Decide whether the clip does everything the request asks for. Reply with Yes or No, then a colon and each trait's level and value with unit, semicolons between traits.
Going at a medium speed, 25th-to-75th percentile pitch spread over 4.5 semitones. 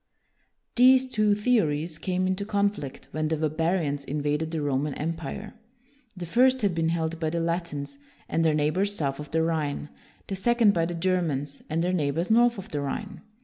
Yes: average, 180 wpm; average, 4.9 semitones